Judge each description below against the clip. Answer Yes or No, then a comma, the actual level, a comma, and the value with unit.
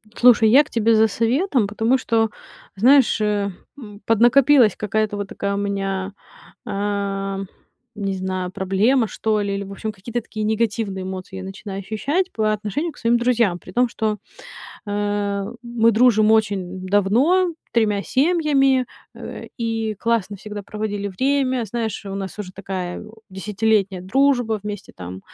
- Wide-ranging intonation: No, average, 3.0 semitones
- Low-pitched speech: No, high, 215 Hz